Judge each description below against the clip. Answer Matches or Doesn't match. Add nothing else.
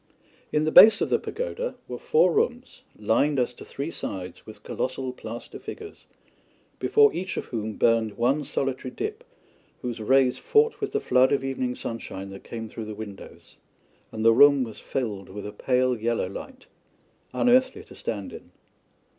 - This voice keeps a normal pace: Matches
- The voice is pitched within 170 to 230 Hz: Doesn't match